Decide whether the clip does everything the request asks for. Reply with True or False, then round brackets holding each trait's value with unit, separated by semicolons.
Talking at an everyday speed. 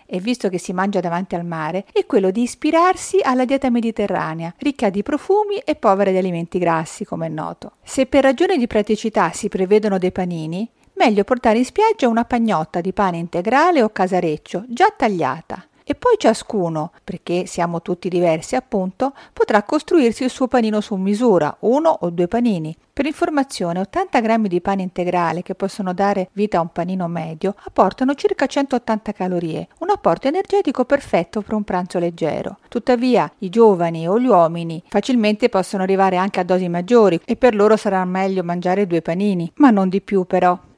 False (175 wpm)